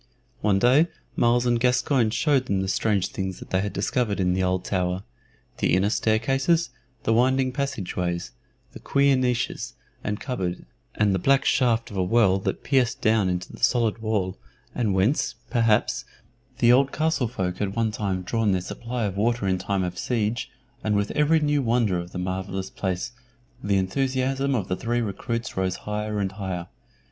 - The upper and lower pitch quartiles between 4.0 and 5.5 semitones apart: Yes, average, 4.7 semitones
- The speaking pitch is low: Yes, low, 110 Hz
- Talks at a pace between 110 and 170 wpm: No, average, 180 wpm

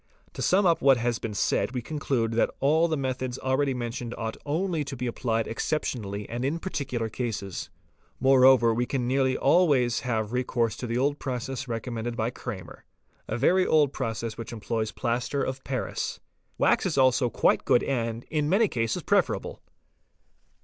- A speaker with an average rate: Yes, average, 170 wpm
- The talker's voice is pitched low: Yes, low, 125 Hz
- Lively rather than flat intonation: No, average, 3.0 semitones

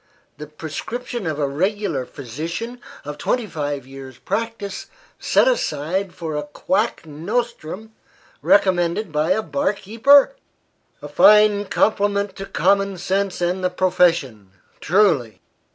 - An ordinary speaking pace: No, slow, 120 wpm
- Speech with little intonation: No, wide, 5.6 semitones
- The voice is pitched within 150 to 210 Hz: Yes, medium, 185 Hz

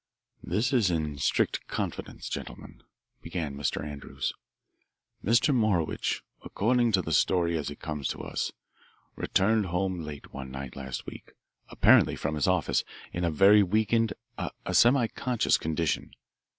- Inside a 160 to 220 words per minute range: No, slow, 135 wpm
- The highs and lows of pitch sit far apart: Yes, wide, 6.6 semitones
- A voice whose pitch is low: Yes, very low, 90 Hz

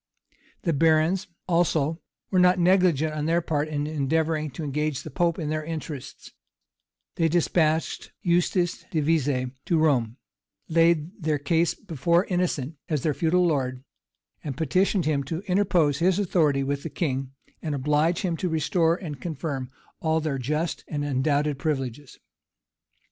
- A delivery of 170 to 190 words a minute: No, average, 150 wpm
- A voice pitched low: No, medium, 155 Hz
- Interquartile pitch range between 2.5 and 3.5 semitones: Yes, average, 2.9 semitones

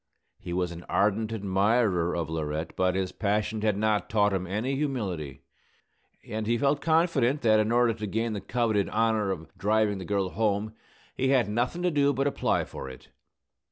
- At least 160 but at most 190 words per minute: Yes, average, 185 wpm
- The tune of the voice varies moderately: Yes, average, 3.6 semitones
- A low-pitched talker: Yes, low, 105 Hz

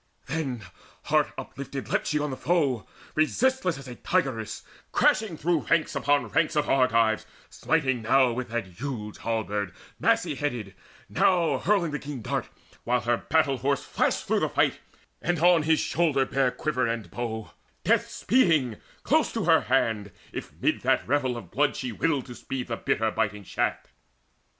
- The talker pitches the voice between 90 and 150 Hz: Yes, low, 135 Hz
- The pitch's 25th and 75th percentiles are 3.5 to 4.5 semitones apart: No, average, 5.1 semitones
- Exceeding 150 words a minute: Yes, average, 165 wpm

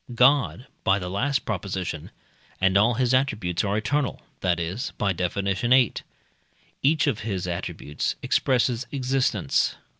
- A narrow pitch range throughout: No, wide, 5.5 semitones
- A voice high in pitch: No, low, 110 Hz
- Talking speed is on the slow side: Yes, slow, 130 wpm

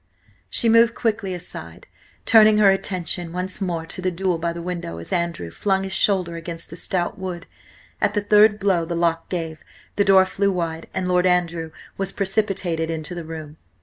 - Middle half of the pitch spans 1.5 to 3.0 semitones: Yes, average, 2.7 semitones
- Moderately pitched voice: Yes, medium, 180 Hz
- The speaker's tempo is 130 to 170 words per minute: No, average, 185 wpm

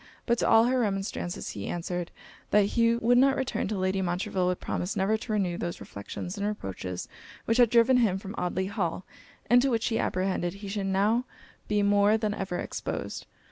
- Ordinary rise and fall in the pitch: Yes, average, 3.6 semitones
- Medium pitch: No, high, 200 Hz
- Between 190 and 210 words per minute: Yes, average, 195 wpm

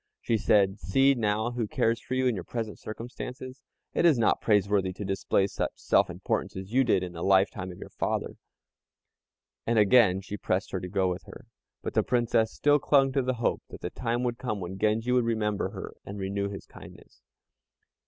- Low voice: Yes, low, 110 Hz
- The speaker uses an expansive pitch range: No, average, 4.1 semitones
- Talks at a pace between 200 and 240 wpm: Yes, fast, 205 wpm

